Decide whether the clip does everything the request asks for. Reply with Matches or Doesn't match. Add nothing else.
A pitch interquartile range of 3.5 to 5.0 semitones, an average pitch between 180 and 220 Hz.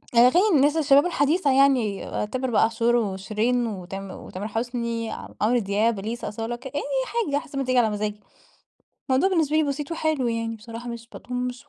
Doesn't match